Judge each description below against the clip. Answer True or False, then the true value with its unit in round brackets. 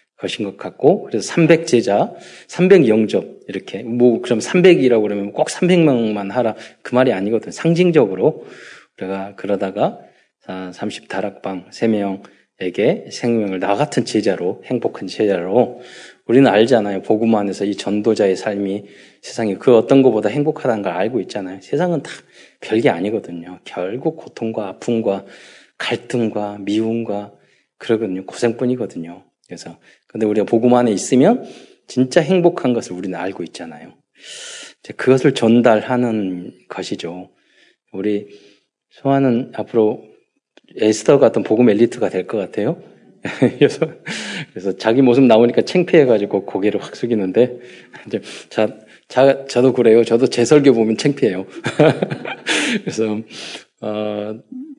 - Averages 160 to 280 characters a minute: False (290 characters per minute)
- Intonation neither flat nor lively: True (3.8 semitones)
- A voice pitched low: True (110 Hz)